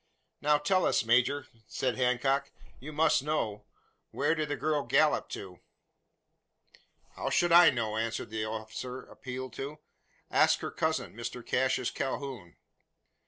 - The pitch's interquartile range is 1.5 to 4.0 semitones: No, average, 4.4 semitones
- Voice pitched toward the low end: Yes, low, 130 Hz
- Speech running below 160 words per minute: Yes, slow, 135 wpm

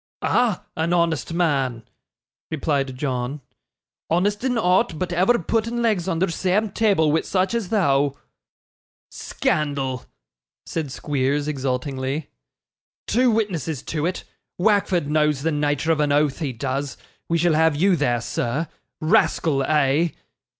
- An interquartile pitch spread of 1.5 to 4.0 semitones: No, average, 4.7 semitones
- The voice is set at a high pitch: No, medium, 160 Hz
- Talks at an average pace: No, slow, 130 wpm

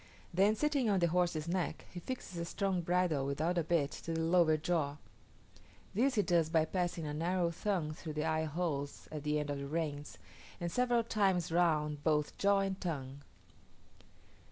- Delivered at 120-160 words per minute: No, average, 180 wpm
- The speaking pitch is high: No, medium, 170 Hz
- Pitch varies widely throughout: No, average, 3.3 semitones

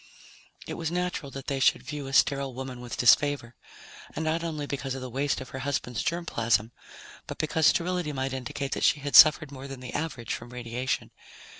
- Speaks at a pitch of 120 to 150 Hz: Yes, low, 135 Hz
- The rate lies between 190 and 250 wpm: Yes, average, 200 wpm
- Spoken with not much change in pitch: No, average, 3.0 semitones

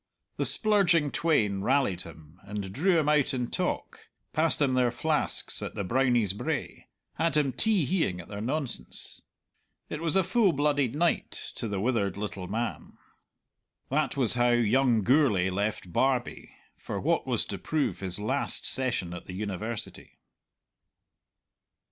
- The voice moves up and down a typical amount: No, wide, 6.7 semitones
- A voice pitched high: No, low, 125 Hz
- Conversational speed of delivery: Yes, average, 150 wpm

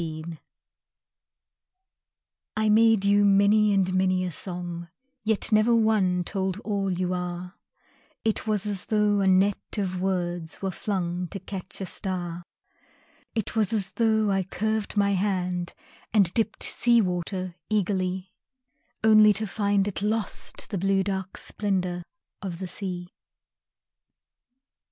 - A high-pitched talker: Yes, high, 195 Hz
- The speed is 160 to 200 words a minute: No, slow, 135 wpm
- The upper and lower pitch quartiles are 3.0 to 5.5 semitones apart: No, narrow, 2.6 semitones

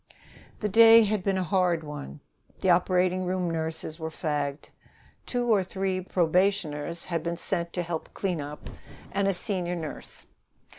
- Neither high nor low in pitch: Yes, medium, 180 Hz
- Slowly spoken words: No, average, 150 wpm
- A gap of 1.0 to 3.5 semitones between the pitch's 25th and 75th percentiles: Yes, average, 3.0 semitones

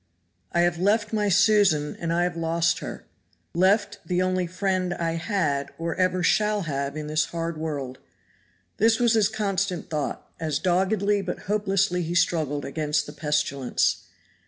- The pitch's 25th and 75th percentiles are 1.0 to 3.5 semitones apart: No, average, 3.9 semitones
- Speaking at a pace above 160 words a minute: No, average, 155 wpm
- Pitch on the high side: No, medium, 175 Hz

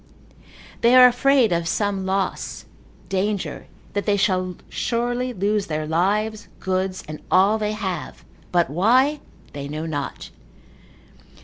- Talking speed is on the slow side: Yes, slow, 125 wpm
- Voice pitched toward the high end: Yes, high, 195 Hz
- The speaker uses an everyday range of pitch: Yes, average, 3.5 semitones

